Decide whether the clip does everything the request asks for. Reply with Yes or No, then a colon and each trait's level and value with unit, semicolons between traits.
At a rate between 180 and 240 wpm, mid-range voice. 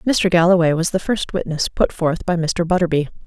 Yes: average, 200 wpm; medium, 175 Hz